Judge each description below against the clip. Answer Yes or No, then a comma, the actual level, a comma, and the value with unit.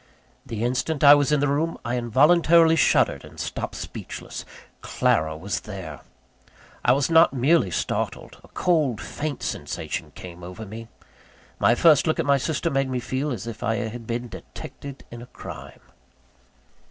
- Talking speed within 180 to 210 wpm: No, average, 165 wpm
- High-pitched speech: No, low, 130 Hz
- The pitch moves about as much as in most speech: Yes, average, 4.8 semitones